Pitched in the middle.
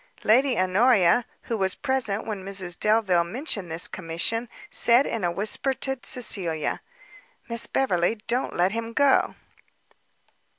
No: high, 215 Hz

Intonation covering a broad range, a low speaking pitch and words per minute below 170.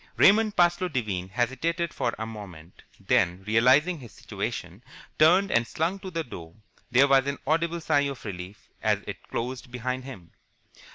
Yes: wide, 7.4 semitones; low, 130 Hz; average, 160 wpm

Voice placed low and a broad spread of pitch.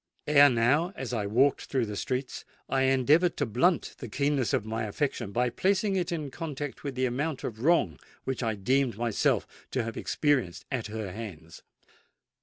No: low, 130 Hz; average, 4.5 semitones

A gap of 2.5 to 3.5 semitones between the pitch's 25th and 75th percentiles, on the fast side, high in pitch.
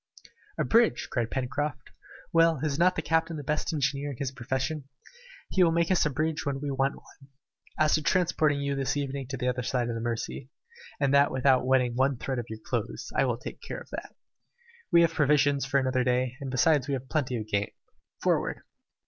No: average, 3.0 semitones; fast, 215 wpm; medium, 140 Hz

